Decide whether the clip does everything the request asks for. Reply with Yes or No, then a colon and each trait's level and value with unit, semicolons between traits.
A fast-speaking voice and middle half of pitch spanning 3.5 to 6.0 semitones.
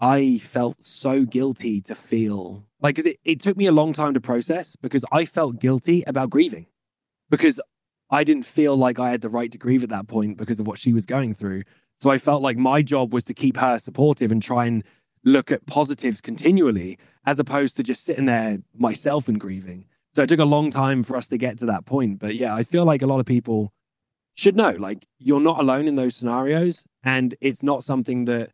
Yes: fast, 225 wpm; average, 3.8 semitones